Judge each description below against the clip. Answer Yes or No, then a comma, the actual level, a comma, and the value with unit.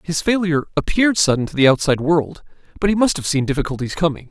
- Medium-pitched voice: Yes, medium, 160 Hz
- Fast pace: Yes, fast, 210 wpm